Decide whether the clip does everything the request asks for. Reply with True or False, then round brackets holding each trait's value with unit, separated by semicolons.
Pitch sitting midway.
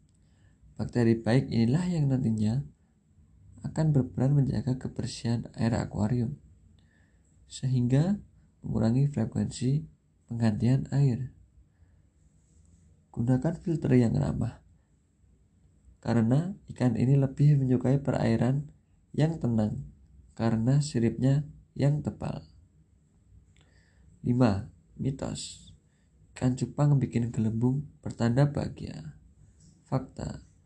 False (115 Hz)